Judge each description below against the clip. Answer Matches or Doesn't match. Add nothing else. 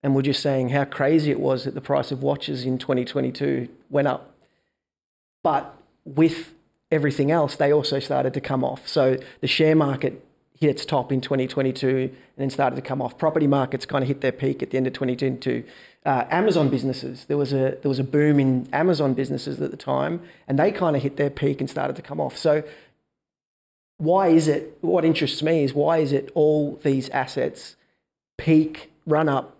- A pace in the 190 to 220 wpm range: Matches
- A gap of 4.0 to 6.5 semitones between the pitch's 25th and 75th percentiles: Doesn't match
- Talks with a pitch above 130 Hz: Matches